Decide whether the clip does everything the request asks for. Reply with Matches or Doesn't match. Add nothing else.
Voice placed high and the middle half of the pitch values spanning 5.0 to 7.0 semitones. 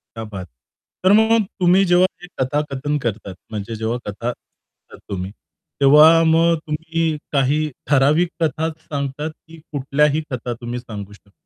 Doesn't match